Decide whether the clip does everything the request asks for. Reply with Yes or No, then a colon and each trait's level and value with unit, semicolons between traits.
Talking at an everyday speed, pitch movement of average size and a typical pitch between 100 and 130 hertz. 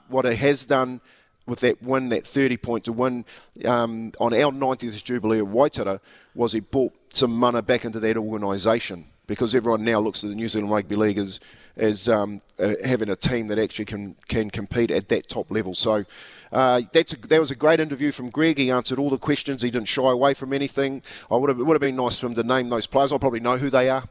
No: fast, 240 wpm; average, 3.4 semitones; low, 120 Hz